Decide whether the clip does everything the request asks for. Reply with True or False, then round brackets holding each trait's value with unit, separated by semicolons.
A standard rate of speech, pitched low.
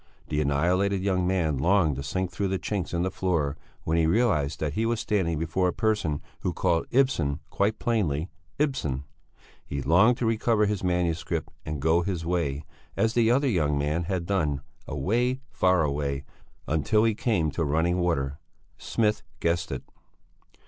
True (170 wpm; 90 Hz)